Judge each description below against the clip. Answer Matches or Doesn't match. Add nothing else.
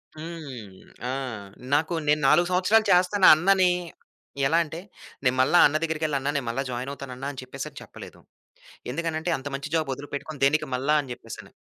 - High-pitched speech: Doesn't match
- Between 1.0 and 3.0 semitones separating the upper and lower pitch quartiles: Doesn't match